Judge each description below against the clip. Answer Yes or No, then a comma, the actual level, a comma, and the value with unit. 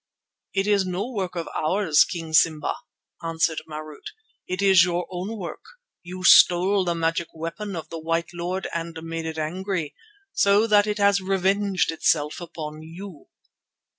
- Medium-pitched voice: Yes, medium, 175 Hz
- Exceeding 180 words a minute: No, average, 155 wpm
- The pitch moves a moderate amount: Yes, average, 3.0 semitones